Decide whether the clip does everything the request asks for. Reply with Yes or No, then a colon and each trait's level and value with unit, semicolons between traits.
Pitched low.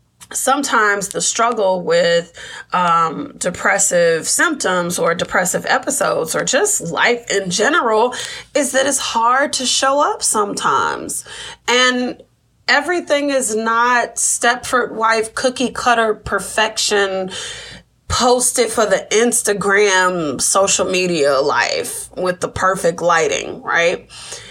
No: high, 225 Hz